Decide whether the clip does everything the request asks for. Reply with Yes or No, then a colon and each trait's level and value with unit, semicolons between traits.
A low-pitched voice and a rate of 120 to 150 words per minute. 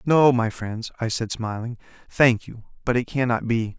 No: low, 120 Hz; fast, 205 wpm